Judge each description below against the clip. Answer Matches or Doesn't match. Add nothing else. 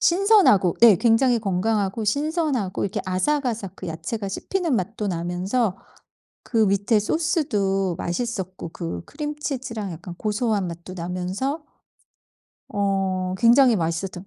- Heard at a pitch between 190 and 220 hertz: Matches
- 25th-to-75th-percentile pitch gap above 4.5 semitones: Matches